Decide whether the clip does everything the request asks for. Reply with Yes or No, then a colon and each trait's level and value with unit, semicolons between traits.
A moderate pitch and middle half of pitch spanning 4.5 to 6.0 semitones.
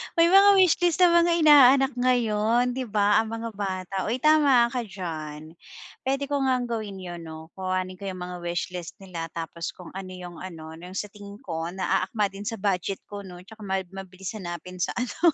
No: high, 200 Hz; wide, 5.4 semitones